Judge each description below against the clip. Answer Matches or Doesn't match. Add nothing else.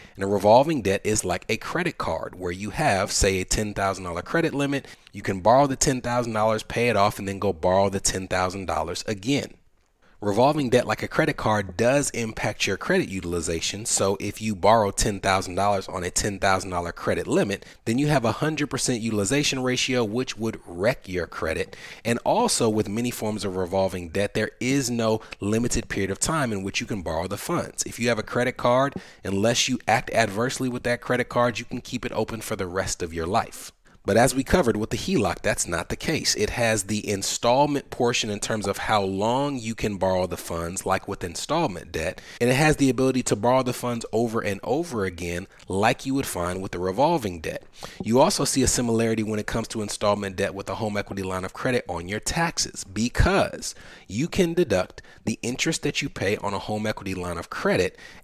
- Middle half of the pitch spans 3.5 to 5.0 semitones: Matches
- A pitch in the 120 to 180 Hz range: Doesn't match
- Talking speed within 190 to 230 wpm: Matches